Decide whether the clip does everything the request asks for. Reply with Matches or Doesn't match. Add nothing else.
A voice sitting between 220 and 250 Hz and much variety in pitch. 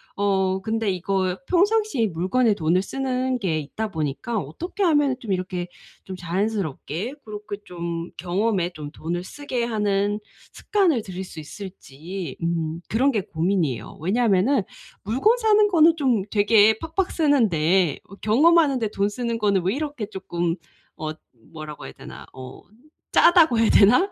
Doesn't match